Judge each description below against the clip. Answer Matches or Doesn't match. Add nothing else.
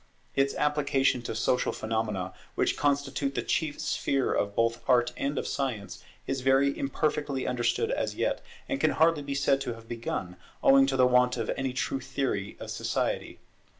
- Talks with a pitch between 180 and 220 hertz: Doesn't match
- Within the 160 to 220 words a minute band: Matches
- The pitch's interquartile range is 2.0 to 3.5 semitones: Matches